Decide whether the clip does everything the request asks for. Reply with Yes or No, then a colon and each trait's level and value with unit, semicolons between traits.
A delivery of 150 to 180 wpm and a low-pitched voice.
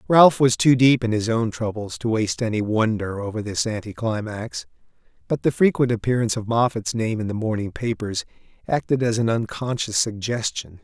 Yes: average, 170 wpm; low, 110 Hz